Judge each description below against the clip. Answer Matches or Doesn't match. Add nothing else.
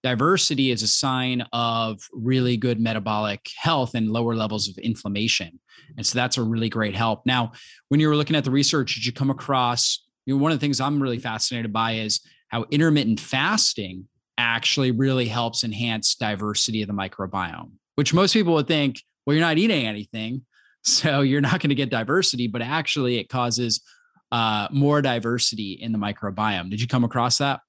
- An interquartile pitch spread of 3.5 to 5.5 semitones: Matches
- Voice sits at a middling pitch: Doesn't match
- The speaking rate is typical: Matches